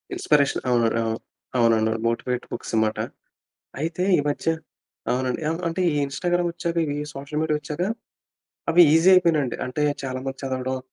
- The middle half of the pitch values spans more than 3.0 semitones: Yes, average, 4.7 semitones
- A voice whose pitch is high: No, medium, 140 Hz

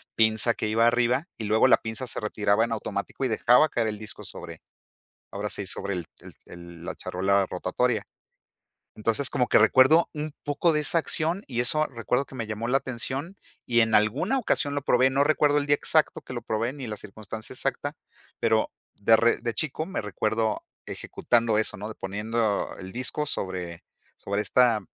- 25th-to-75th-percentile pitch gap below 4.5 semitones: Yes, average, 4.0 semitones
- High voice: No, low, 115 Hz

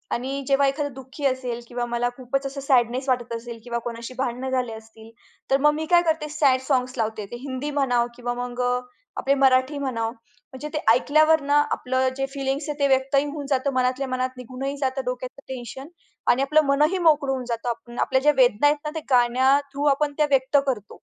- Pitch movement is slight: Yes, narrow, 2.3 semitones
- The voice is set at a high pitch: Yes, very high, 260 Hz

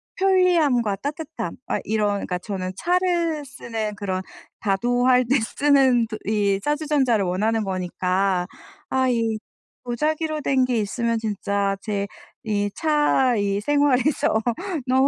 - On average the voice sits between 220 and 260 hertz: Yes, high, 235 Hz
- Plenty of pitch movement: Yes, wide, 6.1 semitones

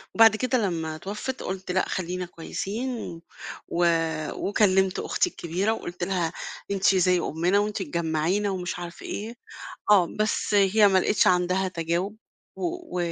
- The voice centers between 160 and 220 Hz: Yes, high, 190 Hz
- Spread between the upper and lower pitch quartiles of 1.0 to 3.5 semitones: Yes, average, 3.0 semitones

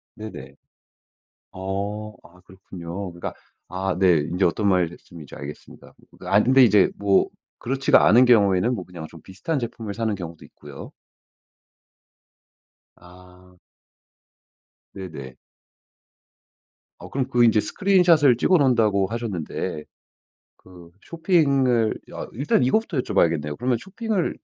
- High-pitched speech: No, low, 100 Hz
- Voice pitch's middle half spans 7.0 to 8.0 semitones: No, wide, 5.8 semitones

